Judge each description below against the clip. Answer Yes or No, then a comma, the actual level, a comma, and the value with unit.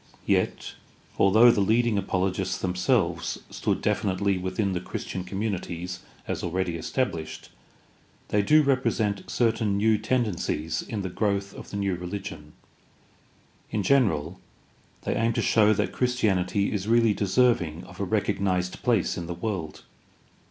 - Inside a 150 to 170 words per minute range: No, slow, 135 wpm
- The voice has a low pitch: Yes, low, 100 Hz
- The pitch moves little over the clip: No, average, 3.3 semitones